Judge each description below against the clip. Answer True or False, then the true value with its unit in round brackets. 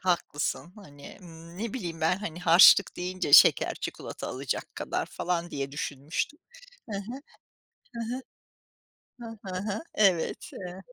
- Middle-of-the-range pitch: True (180 Hz)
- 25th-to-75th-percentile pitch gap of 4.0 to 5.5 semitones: False (3.5 semitones)